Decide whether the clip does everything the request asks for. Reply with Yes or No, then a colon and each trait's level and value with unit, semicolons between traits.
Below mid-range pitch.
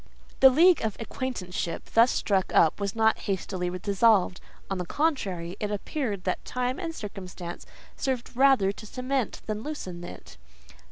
No: high, 210 Hz